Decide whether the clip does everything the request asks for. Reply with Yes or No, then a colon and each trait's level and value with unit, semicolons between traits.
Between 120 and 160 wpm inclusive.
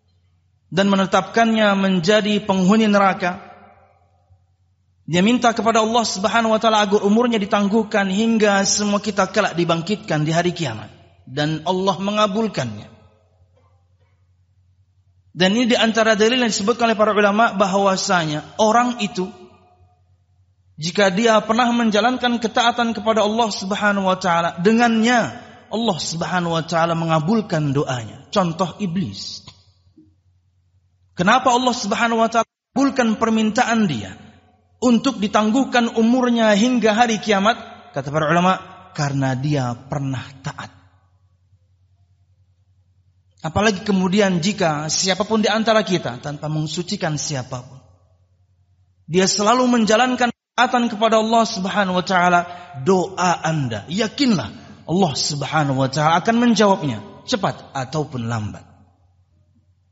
No: average, 110 wpm